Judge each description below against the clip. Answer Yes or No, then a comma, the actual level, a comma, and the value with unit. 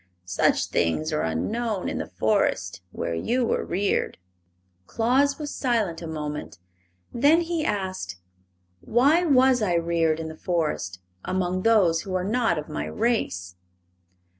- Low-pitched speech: No, medium, 185 Hz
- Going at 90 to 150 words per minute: Yes, average, 140 wpm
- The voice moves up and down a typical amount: No, wide, 7.3 semitones